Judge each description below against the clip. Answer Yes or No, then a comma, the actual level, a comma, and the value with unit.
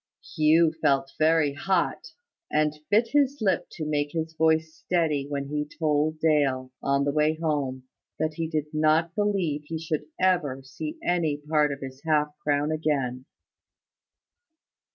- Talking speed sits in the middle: Yes, average, 150 wpm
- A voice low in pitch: No, medium, 155 Hz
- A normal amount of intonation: No, narrow, 2.0 semitones